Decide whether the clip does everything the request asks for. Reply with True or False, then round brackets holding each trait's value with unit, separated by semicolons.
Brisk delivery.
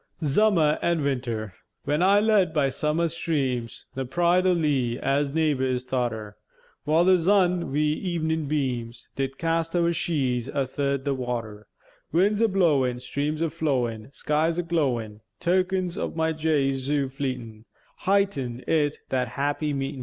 False (155 wpm)